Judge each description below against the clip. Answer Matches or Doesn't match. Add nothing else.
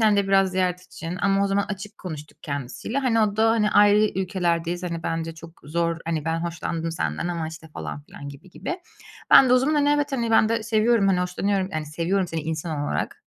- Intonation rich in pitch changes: Doesn't match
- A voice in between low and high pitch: Matches